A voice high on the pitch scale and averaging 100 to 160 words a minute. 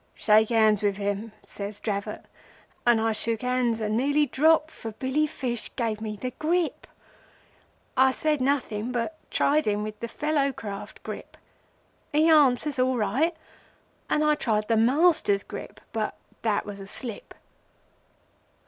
Yes: high, 240 Hz; average, 150 wpm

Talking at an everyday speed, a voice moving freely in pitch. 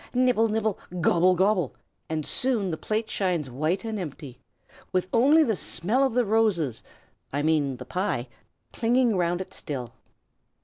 Yes: average, 150 wpm; wide, 6.2 semitones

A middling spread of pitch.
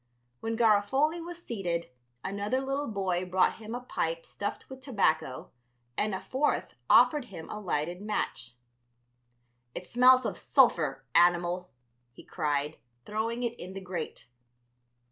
No: wide, 6.2 semitones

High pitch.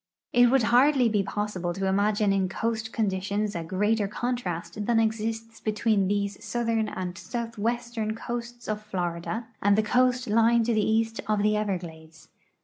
Yes: high, 215 Hz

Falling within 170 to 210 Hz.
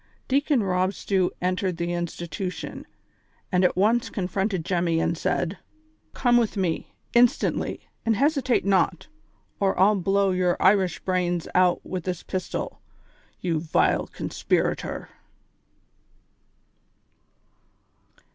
Yes: medium, 185 Hz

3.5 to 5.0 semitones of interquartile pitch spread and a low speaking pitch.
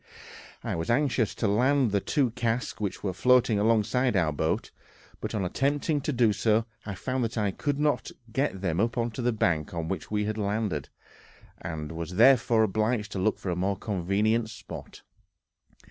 Yes: average, 4.1 semitones; low, 110 Hz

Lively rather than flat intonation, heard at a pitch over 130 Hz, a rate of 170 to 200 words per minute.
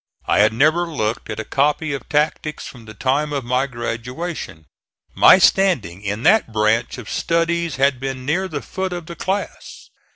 Yes: wide, 6.2 semitones; medium, 140 Hz; average, 175 wpm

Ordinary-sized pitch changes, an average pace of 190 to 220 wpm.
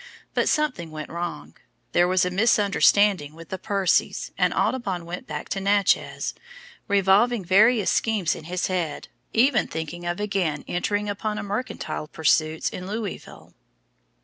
No: average, 3.4 semitones; average, 140 wpm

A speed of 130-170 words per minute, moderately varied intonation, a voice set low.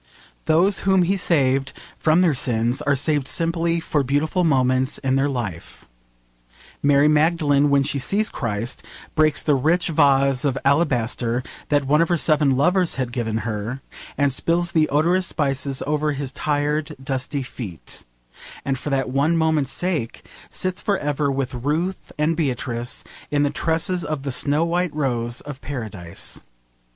No: average, 155 wpm; average, 3.5 semitones; medium, 145 Hz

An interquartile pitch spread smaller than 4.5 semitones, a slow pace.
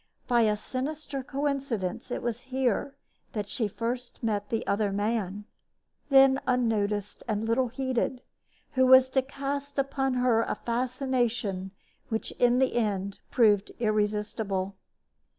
Yes: average, 3.9 semitones; slow, 130 wpm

